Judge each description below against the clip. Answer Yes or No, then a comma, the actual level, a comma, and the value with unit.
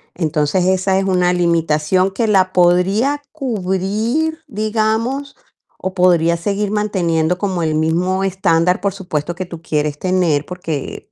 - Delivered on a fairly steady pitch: No, average, 3.2 semitones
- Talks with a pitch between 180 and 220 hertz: Yes, medium, 185 Hz